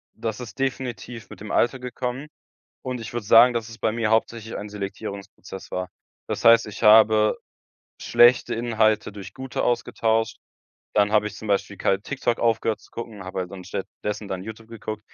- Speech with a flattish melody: Yes, narrow, 2.3 semitones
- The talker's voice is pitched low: Yes, low, 110 Hz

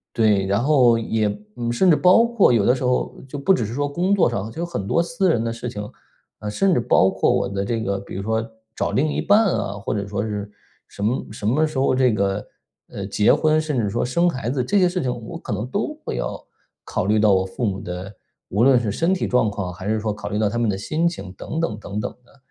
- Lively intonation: Yes, wide, 6.8 semitones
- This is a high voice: No, low, 115 Hz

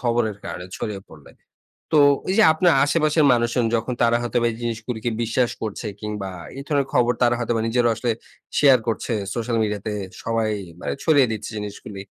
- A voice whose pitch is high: No, low, 120 Hz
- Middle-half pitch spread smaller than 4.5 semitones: Yes, narrow, 2.4 semitones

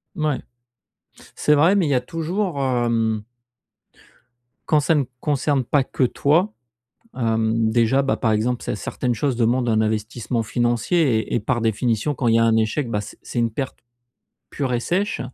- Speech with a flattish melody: No, average, 4.3 semitones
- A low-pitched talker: Yes, low, 125 Hz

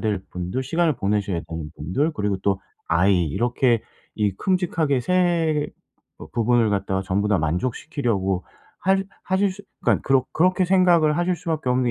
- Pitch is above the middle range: No, low, 125 Hz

